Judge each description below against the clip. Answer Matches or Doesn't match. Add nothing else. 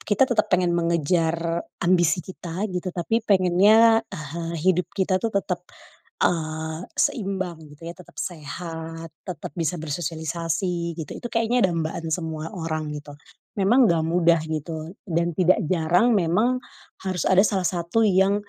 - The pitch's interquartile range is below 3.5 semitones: Matches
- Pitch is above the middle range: Doesn't match